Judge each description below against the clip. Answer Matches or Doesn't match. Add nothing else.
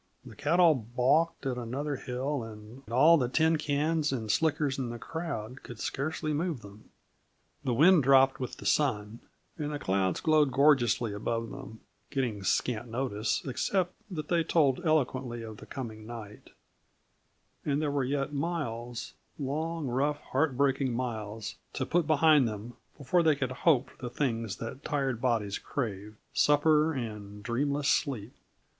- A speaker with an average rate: Matches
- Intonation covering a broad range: Doesn't match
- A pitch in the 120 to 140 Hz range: Matches